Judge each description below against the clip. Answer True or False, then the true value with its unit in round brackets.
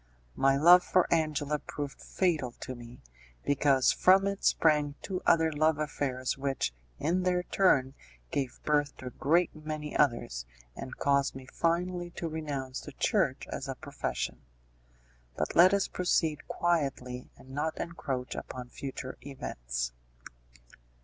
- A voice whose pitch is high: False (145 Hz)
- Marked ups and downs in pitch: False (4.1 semitones)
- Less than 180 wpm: True (140 wpm)